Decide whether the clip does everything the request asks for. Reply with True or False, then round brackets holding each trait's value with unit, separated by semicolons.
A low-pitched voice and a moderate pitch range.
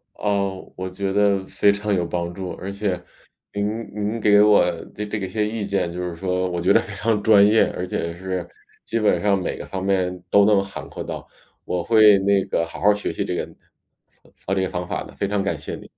False (100 Hz; 2.1 semitones)